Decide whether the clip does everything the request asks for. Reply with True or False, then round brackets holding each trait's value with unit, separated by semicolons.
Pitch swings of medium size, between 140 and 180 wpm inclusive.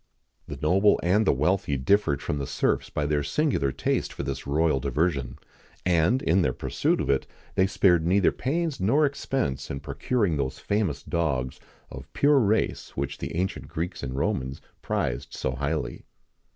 False (6.2 semitones; 175 wpm)